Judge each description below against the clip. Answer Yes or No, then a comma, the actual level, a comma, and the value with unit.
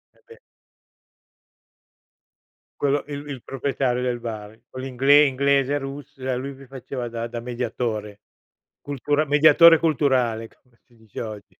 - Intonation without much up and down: No, average, 3.1 semitones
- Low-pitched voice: Yes, low, 130 Hz